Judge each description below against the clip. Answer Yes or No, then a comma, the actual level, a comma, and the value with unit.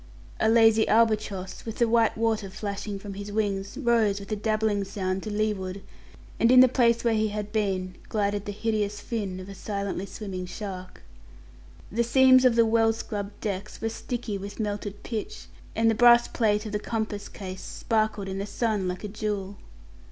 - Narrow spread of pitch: Yes, narrow, 2.1 semitones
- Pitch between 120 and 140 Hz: No, high, 210 Hz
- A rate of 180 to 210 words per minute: Yes, average, 185 wpm